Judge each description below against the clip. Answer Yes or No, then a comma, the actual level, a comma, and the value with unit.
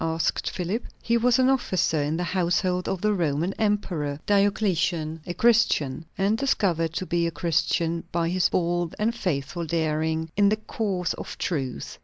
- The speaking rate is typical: Yes, average, 165 wpm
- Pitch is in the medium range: Yes, medium, 175 Hz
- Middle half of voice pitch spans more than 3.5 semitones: Yes, average, 4.0 semitones